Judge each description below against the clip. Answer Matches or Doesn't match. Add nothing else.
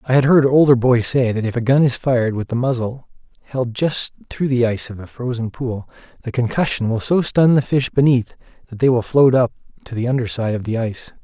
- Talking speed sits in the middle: Doesn't match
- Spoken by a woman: Doesn't match